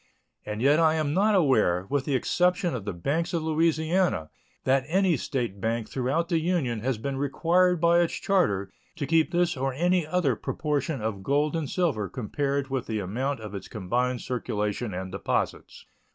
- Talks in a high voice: No, medium, 140 Hz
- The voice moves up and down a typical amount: No, wide, 6.6 semitones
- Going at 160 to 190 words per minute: Yes, average, 180 wpm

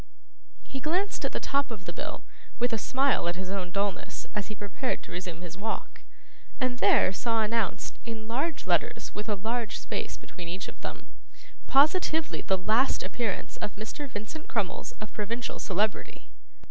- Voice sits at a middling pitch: No, high, 220 Hz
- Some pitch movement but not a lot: Yes, average, 4.5 semitones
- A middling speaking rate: Yes, average, 170 wpm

